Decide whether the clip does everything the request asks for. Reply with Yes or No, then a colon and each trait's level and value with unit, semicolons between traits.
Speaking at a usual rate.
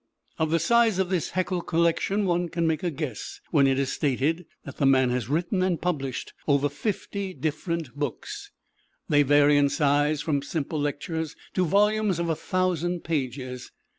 Yes: average, 170 wpm